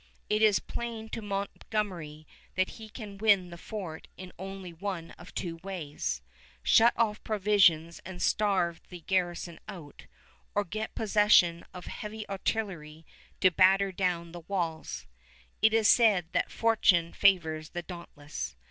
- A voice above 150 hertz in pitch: Yes, medium, 185 Hz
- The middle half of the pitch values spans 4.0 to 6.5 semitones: No, average, 3.6 semitones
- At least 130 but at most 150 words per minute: Yes, average, 140 wpm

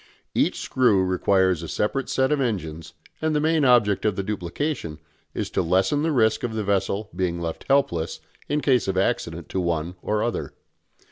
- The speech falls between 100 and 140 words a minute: No, average, 185 wpm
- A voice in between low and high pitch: No, low, 100 Hz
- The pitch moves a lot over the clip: Yes, wide, 6.4 semitones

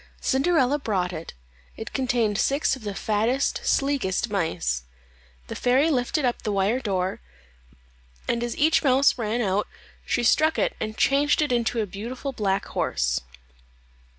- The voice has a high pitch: Yes, high, 235 Hz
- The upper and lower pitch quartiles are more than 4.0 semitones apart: Yes, average, 5.2 semitones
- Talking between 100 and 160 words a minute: Yes, average, 150 wpm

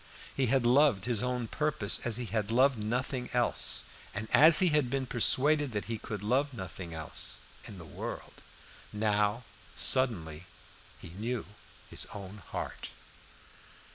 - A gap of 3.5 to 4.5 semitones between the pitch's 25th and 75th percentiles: Yes, average, 4.2 semitones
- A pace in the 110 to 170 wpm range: Yes, average, 150 wpm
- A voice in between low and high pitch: No, low, 115 Hz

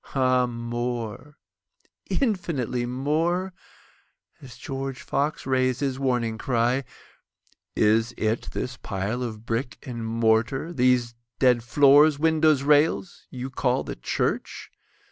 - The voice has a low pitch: Yes, low, 125 Hz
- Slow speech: Yes, slow, 95 wpm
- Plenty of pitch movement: No, average, 3.2 semitones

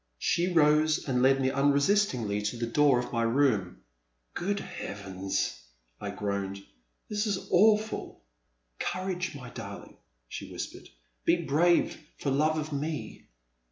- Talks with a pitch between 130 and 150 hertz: Yes, medium, 140 Hz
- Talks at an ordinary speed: No, slow, 130 wpm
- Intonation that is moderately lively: No, wide, 7.9 semitones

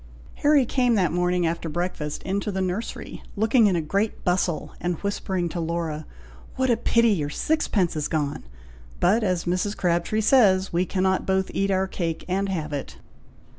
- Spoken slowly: No, average, 170 wpm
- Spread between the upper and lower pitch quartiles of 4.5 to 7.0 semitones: No, average, 3.3 semitones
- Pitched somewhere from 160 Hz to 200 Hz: Yes, medium, 185 Hz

